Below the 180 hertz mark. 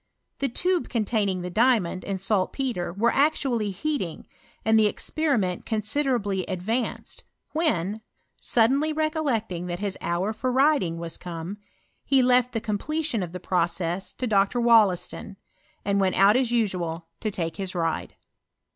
No: high, 210 Hz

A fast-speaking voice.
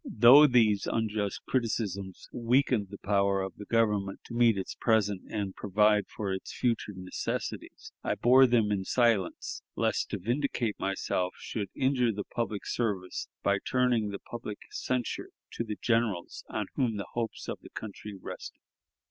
No: average, 155 wpm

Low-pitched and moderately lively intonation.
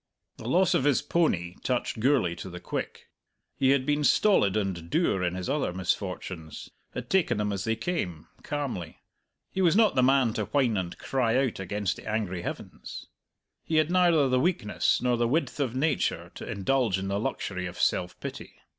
No: low, 115 Hz; wide, 7.4 semitones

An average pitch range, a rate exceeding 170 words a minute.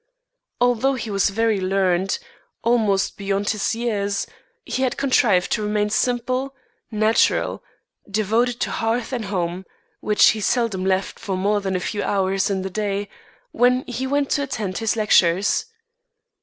No: average, 3.6 semitones; average, 150 wpm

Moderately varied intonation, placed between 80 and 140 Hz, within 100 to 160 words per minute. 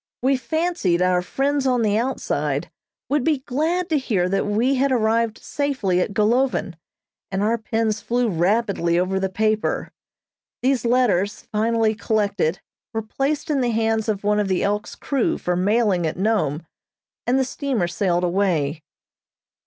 No: average, 4.9 semitones; high, 220 Hz; average, 155 wpm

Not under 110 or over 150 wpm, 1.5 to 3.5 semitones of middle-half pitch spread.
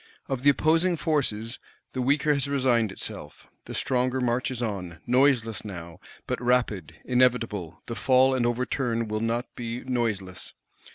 Yes: average, 140 wpm; average, 2.8 semitones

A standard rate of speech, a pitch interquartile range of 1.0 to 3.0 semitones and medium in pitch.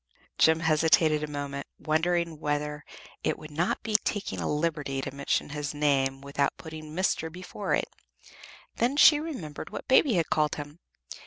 Yes: average, 160 wpm; average, 2.7 semitones; medium, 155 Hz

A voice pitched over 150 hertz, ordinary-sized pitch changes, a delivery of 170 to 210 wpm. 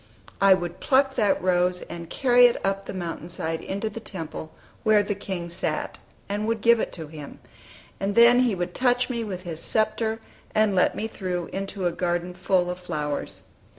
Yes: high, 190 Hz; average, 3.8 semitones; average, 190 wpm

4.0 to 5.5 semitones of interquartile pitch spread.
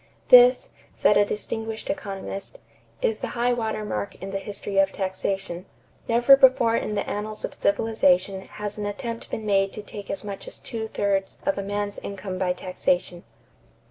No: narrow, 2.6 semitones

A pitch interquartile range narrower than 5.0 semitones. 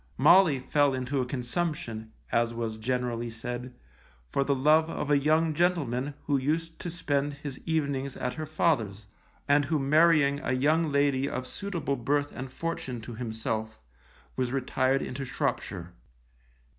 Yes: average, 3.5 semitones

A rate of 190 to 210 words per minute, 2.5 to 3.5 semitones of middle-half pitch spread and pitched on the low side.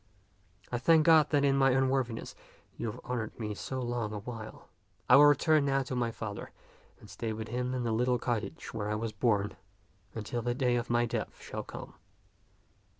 Yes: average, 200 wpm; average, 3.0 semitones; low, 120 Hz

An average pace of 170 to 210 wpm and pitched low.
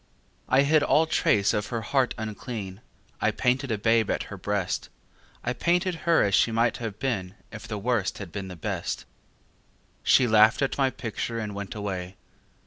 Yes: average, 180 wpm; low, 110 Hz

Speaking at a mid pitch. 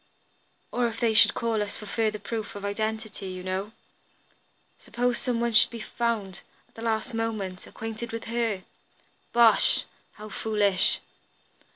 No: high, 220 Hz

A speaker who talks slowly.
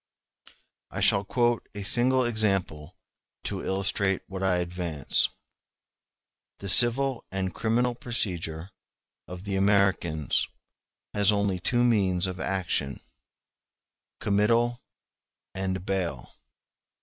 Yes: slow, 95 wpm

